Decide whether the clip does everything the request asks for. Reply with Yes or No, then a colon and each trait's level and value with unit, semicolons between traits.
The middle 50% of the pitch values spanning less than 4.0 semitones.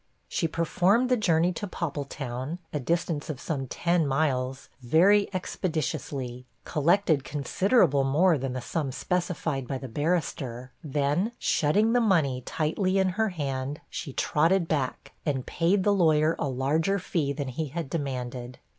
No: average, 4.9 semitones